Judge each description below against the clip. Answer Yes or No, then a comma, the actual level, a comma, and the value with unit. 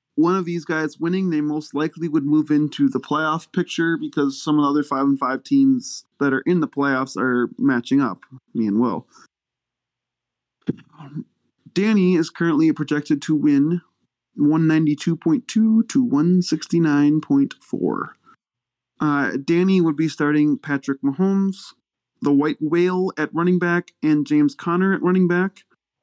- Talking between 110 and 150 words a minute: Yes, average, 145 wpm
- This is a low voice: No, medium, 155 Hz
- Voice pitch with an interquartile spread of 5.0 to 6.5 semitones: No, average, 4.1 semitones